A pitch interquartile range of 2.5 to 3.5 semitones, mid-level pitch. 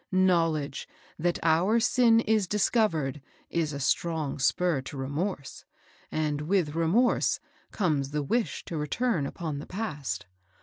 No: average, 5.3 semitones; medium, 165 Hz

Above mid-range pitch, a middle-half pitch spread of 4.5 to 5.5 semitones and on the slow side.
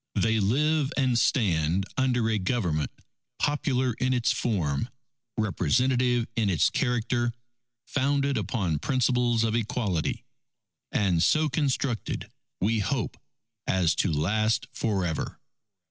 No: low, 115 Hz; average, 5.1 semitones; slow, 115 wpm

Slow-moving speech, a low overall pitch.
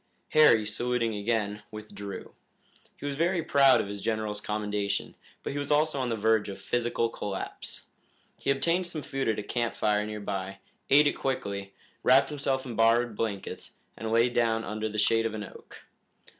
No: average, 180 wpm; low, 115 Hz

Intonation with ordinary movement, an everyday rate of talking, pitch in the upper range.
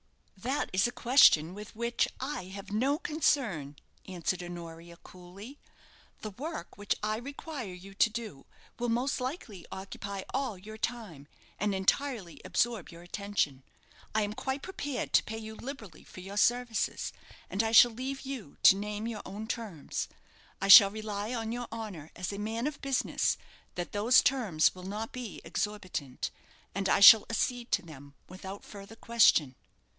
Yes: average, 4.2 semitones; average, 160 wpm; high, 210 Hz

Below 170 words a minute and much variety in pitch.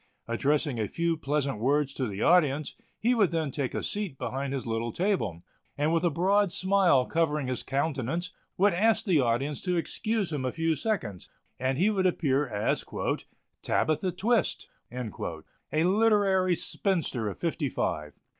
Yes: average, 160 wpm; wide, 6.1 semitones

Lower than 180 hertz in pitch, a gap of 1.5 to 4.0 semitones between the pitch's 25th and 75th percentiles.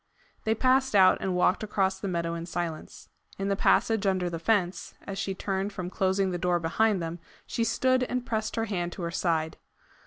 No: high, 190 Hz; average, 3.6 semitones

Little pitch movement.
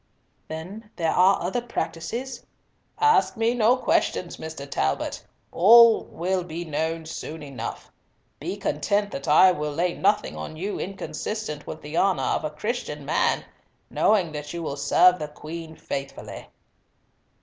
No: average, 5.1 semitones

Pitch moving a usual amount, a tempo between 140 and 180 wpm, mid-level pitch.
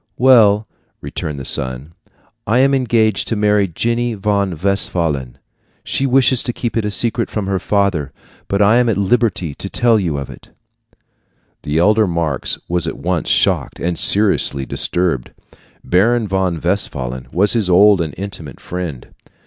No: average, 4.9 semitones; average, 155 wpm; low, 100 Hz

